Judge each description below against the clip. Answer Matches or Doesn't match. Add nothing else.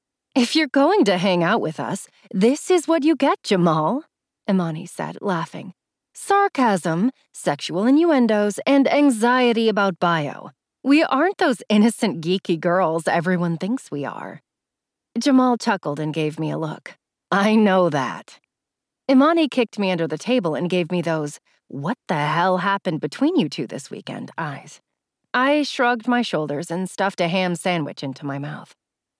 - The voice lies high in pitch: Matches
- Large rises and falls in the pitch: Matches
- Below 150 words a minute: Doesn't match